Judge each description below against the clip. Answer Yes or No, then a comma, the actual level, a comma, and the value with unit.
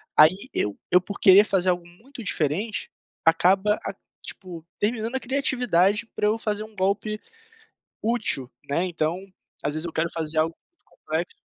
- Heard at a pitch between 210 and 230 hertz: No, high, 190 Hz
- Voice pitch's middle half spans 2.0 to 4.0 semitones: No, average, 4.5 semitones